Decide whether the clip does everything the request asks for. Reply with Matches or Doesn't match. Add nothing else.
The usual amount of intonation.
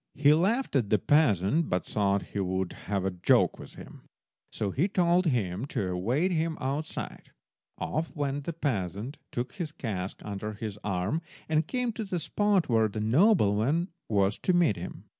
Doesn't match